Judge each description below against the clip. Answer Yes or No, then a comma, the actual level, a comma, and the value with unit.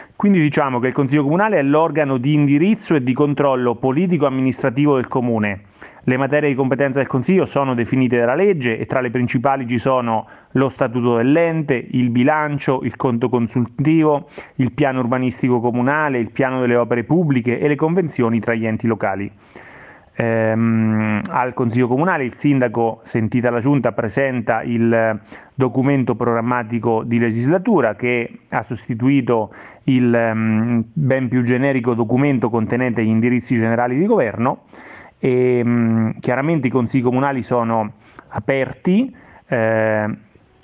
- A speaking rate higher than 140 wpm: No, average, 135 wpm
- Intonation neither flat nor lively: Yes, average, 3.0 semitones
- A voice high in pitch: No, low, 125 Hz